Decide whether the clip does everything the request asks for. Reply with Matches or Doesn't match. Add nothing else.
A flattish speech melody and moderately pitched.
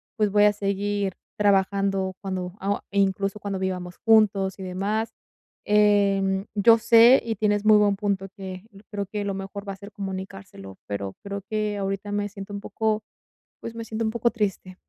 Doesn't match